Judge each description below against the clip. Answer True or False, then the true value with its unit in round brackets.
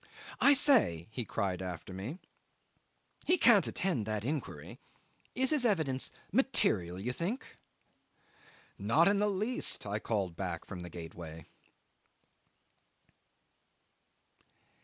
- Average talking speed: False (110 wpm)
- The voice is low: True (125 Hz)